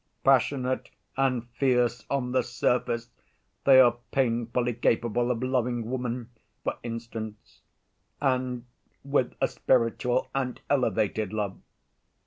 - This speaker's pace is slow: Yes, slow, 110 wpm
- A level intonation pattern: Yes, narrow, 1.8 semitones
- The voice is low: Yes, low, 125 Hz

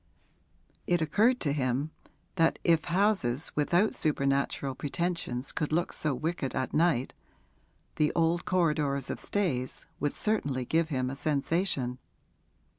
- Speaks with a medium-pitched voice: Yes, medium, 155 Hz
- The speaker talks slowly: Yes, slow, 125 wpm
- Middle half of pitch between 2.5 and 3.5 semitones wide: No, average, 4.0 semitones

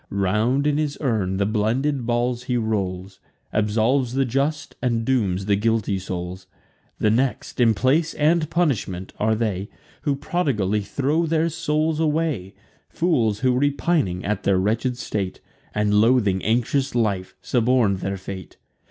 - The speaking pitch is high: No, low, 115 Hz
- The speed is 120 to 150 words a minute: Yes, average, 145 wpm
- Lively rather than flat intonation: Yes, wide, 5.8 semitones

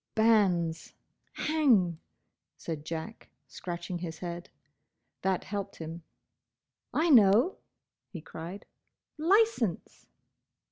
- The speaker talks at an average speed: No, slow, 85 wpm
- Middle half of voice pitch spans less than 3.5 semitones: No, average, 5.1 semitones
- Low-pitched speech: No, medium, 185 Hz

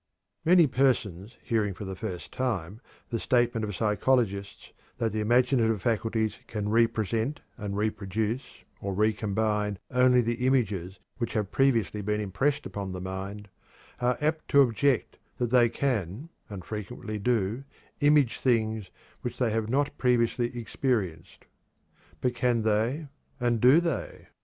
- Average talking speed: Yes, average, 145 wpm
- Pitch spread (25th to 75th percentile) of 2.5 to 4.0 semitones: Yes, average, 3.3 semitones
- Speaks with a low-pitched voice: Yes, low, 115 Hz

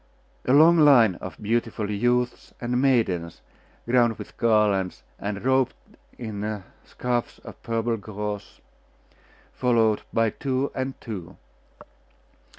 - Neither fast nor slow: No, slow, 110 wpm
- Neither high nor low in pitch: No, low, 115 Hz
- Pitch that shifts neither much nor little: Yes, average, 3.1 semitones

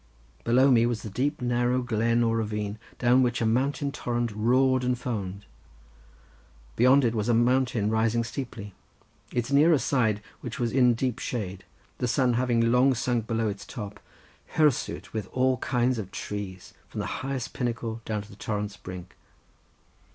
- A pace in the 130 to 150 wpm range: No, average, 165 wpm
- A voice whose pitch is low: Yes, low, 120 Hz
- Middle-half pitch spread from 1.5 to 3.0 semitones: Yes, average, 2.7 semitones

